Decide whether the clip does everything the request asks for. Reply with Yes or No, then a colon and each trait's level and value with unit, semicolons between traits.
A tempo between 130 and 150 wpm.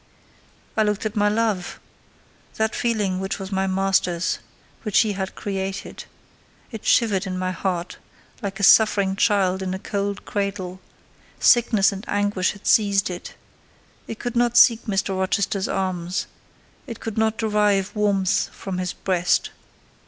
Yes: average, 140 wpm